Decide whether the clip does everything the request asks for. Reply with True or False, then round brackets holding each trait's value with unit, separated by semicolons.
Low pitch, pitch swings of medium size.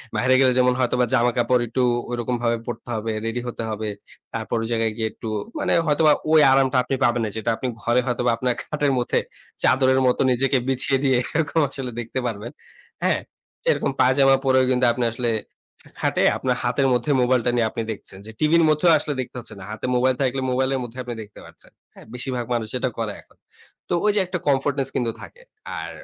False (125 Hz; 2.1 semitones)